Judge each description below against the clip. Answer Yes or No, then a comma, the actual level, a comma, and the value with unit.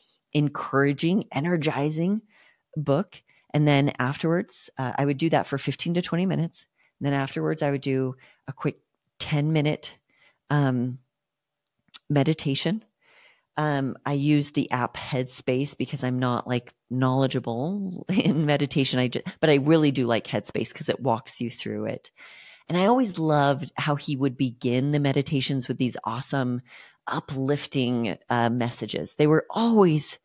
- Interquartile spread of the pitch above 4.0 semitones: No, average, 3.4 semitones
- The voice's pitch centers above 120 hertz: Yes, medium, 140 Hz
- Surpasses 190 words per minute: No, average, 145 wpm